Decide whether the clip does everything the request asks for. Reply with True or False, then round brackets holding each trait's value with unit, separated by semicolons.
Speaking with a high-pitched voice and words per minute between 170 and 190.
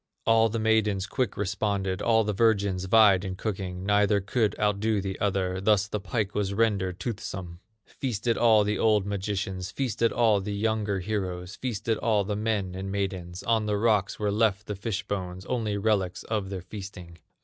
False (100 Hz; 175 wpm)